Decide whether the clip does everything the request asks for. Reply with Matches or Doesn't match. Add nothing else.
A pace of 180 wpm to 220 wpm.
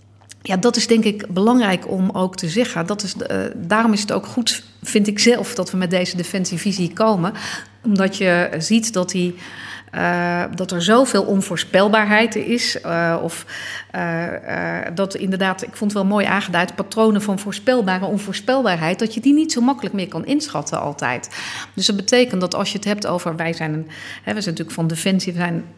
Matches